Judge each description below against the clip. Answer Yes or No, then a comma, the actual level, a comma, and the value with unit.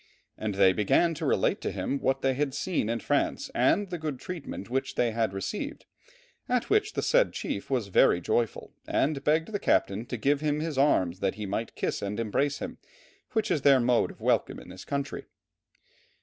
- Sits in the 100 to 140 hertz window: Yes, low, 135 Hz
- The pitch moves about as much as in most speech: No, wide, 6.4 semitones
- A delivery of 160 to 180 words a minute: No, average, 200 wpm